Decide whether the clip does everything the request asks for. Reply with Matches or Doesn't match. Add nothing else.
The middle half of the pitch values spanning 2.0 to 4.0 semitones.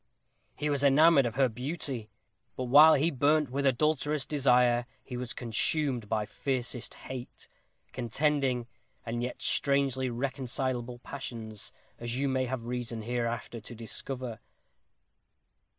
Matches